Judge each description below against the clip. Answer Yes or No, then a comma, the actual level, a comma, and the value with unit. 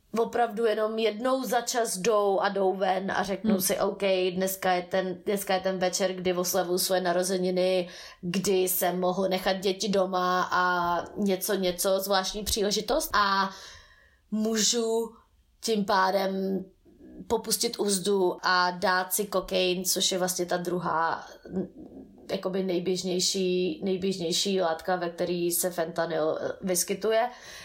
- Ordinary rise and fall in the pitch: No, narrow, 1.9 semitones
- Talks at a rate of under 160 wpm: Yes, average, 130 wpm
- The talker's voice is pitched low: No, high, 190 Hz